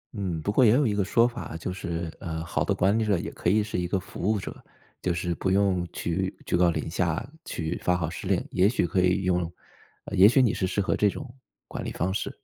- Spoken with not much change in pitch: No, average, 3.0 semitones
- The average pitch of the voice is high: No, very low, 95 Hz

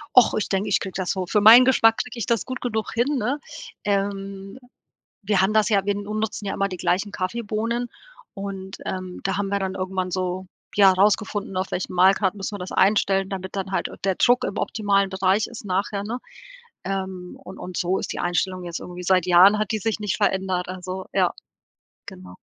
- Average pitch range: No, narrow, 2.2 semitones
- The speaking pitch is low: No, high, 195 Hz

